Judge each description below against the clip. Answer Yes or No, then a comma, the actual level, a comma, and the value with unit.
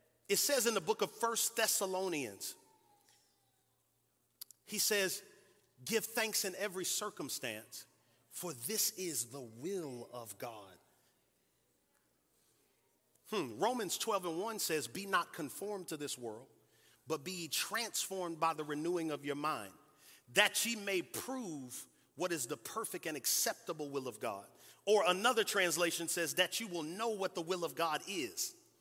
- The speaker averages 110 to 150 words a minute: Yes, average, 145 wpm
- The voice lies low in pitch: No, medium, 185 Hz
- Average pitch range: No, wide, 6.1 semitones